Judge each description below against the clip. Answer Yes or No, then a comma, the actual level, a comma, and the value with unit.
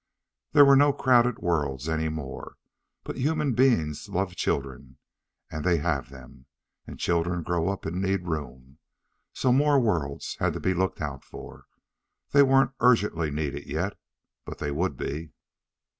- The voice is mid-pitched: No, very low, 85 Hz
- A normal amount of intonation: No, wide, 8.7 semitones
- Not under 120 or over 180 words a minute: Yes, average, 155 wpm